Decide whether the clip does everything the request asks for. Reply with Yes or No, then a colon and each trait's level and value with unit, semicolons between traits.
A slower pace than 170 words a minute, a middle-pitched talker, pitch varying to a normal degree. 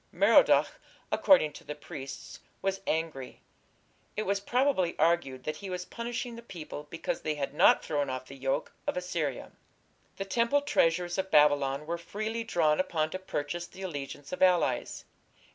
Yes: average, 160 wpm; medium, 170 Hz; average, 4.9 semitones